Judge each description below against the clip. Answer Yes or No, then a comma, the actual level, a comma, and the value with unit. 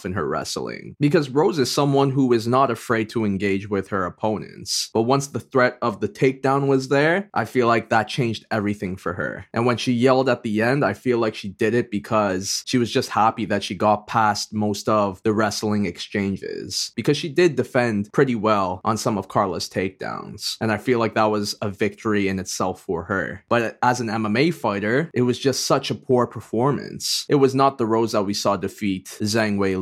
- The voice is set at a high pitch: No, low, 115 Hz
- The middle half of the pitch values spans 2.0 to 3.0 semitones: No, average, 3.7 semitones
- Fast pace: Yes, fast, 215 wpm